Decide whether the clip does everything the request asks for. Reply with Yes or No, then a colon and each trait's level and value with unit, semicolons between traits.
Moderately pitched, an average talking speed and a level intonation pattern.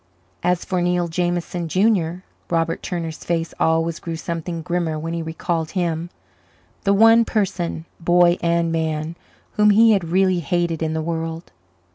Yes: medium, 170 Hz; average, 150 wpm; narrow, 1.6 semitones